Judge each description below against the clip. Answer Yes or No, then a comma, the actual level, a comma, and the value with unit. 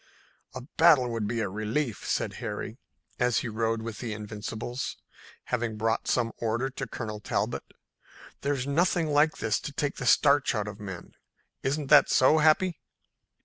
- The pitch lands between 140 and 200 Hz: No, low, 120 Hz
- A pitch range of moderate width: Yes, average, 4.7 semitones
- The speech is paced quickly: No, average, 160 wpm